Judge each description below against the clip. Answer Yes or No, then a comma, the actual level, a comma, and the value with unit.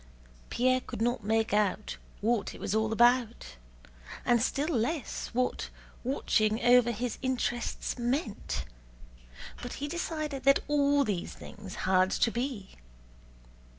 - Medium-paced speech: No, slow, 125 wpm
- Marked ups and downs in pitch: No, average, 3.3 semitones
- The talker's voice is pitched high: Yes, high, 240 Hz